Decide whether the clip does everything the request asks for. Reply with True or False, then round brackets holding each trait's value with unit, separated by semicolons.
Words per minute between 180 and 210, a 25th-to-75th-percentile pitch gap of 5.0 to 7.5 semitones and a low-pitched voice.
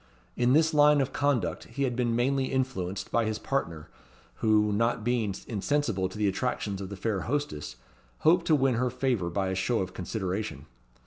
True (185 wpm; 5.6 semitones; 115 Hz)